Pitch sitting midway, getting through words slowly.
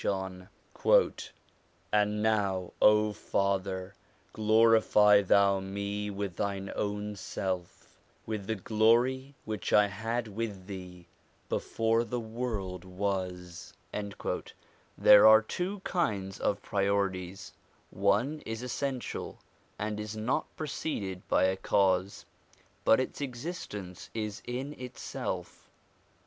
No: low, 105 Hz; slow, 105 wpm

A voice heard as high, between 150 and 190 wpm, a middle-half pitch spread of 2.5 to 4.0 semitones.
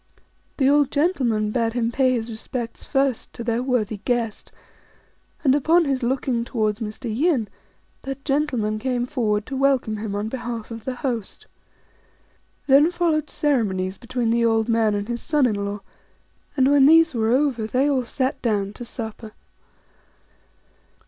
Yes: high, 240 Hz; average, 155 wpm; average, 3.7 semitones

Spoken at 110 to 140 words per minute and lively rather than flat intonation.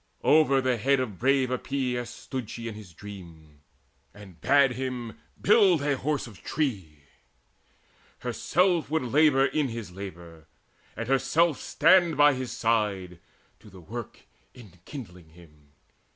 Yes: slow, 135 wpm; wide, 6.5 semitones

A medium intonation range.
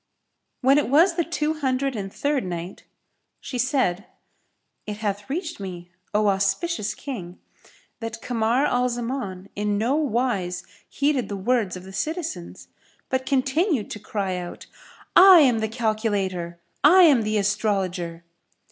No: wide, 6.0 semitones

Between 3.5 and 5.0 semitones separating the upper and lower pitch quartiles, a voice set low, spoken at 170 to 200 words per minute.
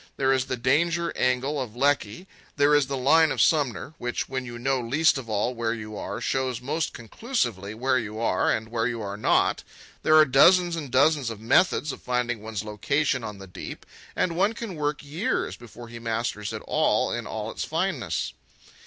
Yes: average, 4.7 semitones; low, 130 Hz; average, 195 wpm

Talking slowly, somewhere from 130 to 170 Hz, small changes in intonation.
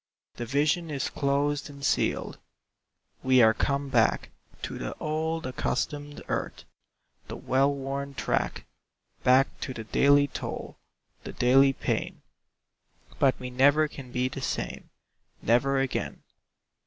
Yes: slow, 130 wpm; medium, 140 Hz; narrow, 1.9 semitones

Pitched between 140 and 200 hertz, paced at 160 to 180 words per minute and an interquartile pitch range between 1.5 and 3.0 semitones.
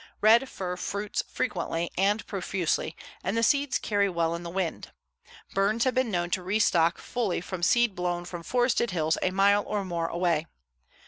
No: high, 190 Hz; average, 175 wpm; average, 3.5 semitones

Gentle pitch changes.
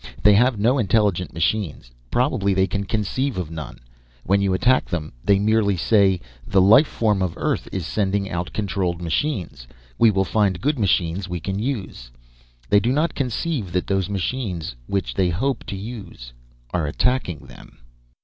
No: average, 3.9 semitones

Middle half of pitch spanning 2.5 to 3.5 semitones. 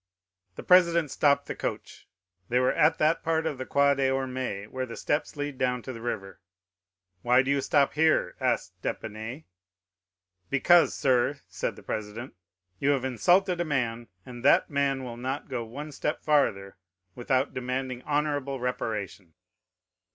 Yes: average, 3.2 semitones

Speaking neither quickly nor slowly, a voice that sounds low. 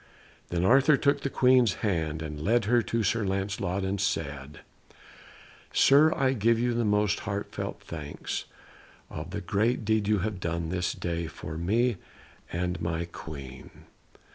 Yes: average, 150 wpm; low, 100 Hz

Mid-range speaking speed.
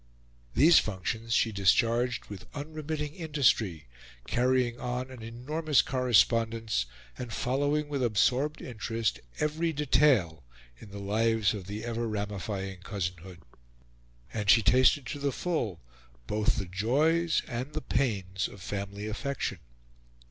No: slow, 125 wpm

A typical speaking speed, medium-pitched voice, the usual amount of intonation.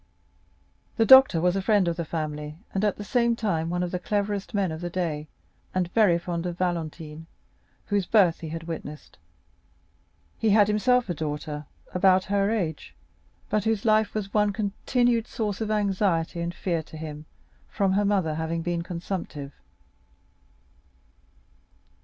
Yes: average, 160 wpm; medium, 180 Hz; average, 4.1 semitones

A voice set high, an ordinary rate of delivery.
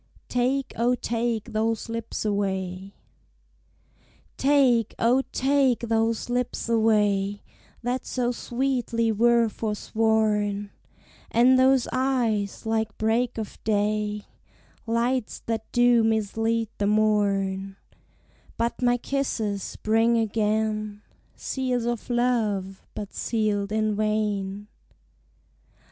No: high, 225 Hz; slow, 95 wpm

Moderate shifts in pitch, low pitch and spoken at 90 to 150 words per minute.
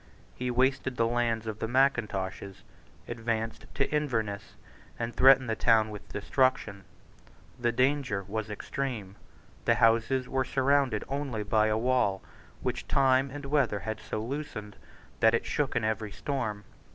Yes: average, 3.5 semitones; low, 115 Hz; average, 145 wpm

